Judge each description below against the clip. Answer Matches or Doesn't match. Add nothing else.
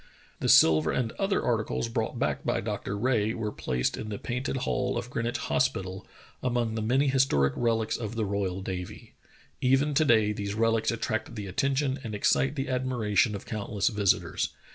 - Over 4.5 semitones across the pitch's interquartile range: Doesn't match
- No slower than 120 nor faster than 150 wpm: Doesn't match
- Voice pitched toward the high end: Doesn't match